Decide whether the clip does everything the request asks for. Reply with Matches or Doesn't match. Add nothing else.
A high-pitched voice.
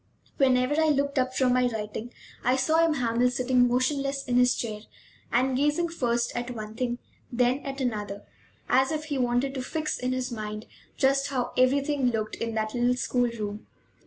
Matches